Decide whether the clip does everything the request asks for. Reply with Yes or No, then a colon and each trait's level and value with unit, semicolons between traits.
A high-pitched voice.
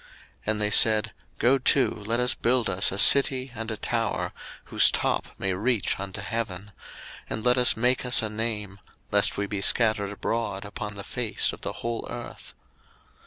No: low, 110 Hz